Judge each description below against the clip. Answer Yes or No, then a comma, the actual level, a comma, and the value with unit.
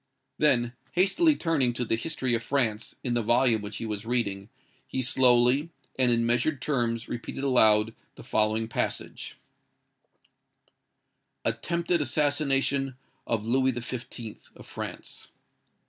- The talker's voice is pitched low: Yes, low, 120 Hz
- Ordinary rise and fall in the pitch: Yes, average, 3.1 semitones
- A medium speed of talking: No, slow, 125 wpm